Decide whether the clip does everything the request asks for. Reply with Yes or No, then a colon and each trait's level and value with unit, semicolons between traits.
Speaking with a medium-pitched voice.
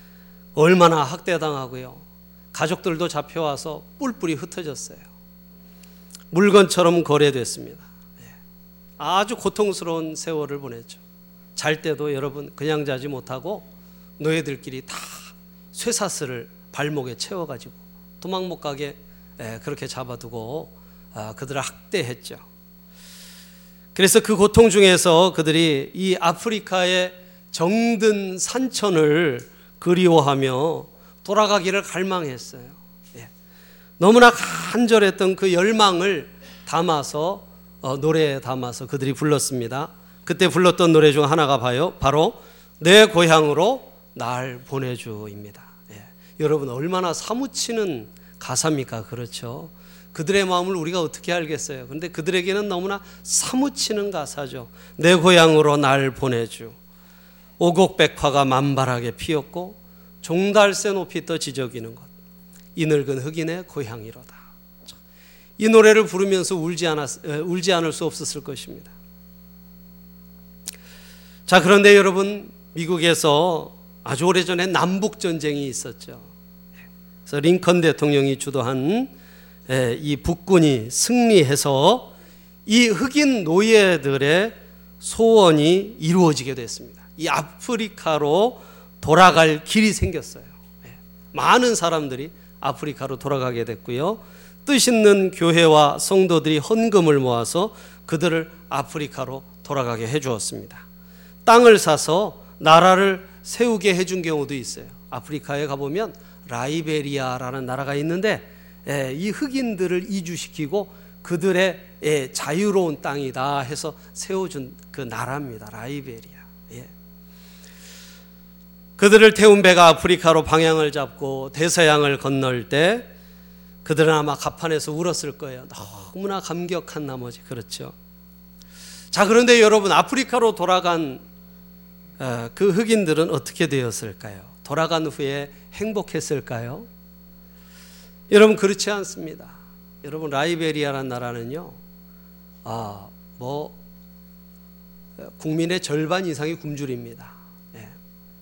Yes: medium, 160 Hz